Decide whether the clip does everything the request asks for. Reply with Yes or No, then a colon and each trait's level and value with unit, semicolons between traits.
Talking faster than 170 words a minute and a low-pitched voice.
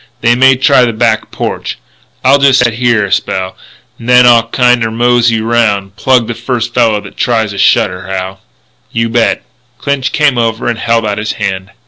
Yes: average, 185 wpm; low, 115 Hz